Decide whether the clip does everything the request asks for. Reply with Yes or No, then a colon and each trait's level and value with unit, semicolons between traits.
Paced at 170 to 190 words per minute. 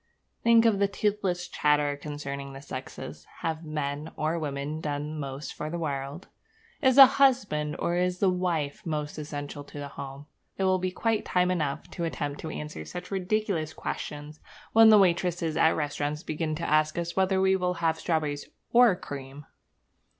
Yes: average, 175 wpm